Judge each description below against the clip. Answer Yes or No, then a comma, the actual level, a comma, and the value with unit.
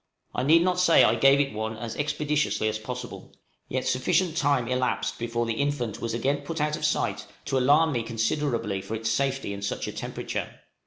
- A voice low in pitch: Yes, low, 130 Hz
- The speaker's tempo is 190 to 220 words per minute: Yes, average, 200 wpm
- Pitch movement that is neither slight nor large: Yes, average, 4.3 semitones